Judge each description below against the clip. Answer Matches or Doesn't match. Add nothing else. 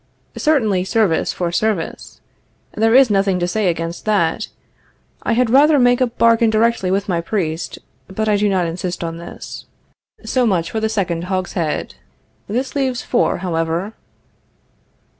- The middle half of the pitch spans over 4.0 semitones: Matches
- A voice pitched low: Doesn't match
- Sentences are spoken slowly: Doesn't match